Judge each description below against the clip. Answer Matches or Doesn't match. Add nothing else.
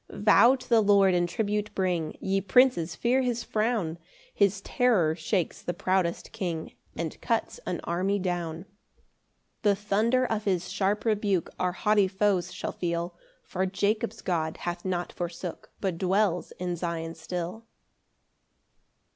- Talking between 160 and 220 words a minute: Doesn't match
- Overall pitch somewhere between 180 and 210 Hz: Matches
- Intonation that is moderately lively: Matches